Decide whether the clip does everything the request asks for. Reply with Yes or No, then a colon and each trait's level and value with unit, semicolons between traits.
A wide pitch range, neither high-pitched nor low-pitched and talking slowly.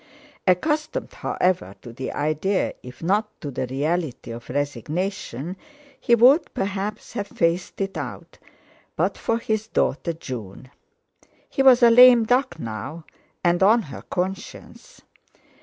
Yes: wide, 7.3 semitones; medium, 180 Hz; slow, 130 wpm